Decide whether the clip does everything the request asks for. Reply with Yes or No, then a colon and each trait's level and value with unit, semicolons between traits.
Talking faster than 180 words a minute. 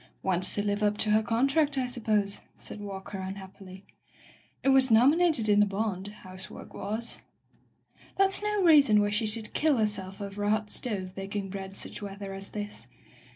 Yes: average, 190 wpm